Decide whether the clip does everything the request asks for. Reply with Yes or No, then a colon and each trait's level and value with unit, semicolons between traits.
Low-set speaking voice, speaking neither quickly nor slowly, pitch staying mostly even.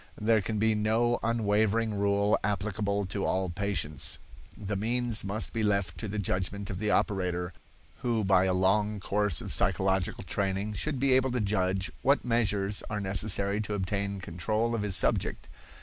Yes: low, 100 Hz; average, 165 wpm; narrow, 2.1 semitones